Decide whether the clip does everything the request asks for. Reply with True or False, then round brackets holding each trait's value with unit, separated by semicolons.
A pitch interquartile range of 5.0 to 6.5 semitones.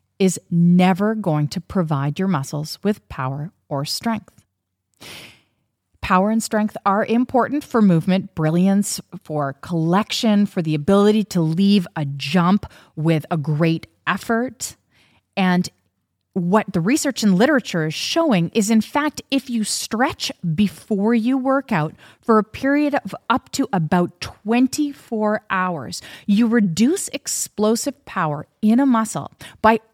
True (5.4 semitones)